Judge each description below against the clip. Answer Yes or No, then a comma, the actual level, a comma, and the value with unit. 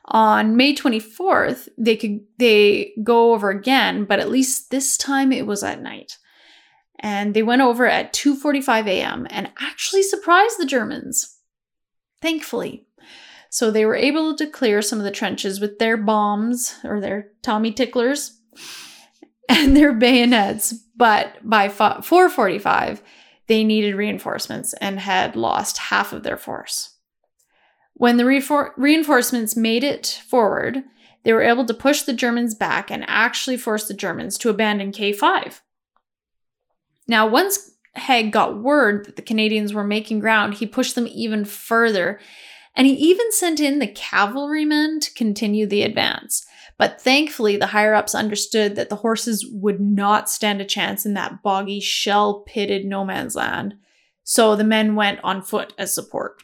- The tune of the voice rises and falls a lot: No, average, 4.5 semitones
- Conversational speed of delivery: Yes, average, 150 wpm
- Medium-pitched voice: No, high, 230 Hz